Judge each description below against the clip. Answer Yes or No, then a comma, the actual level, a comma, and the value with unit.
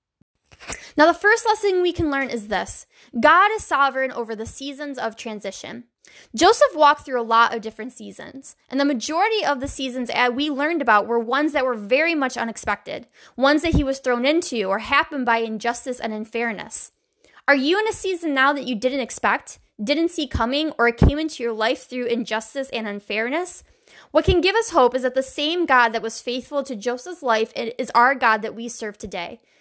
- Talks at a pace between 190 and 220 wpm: Yes, average, 200 wpm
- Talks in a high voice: Yes, very high, 260 Hz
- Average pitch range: Yes, average, 4.5 semitones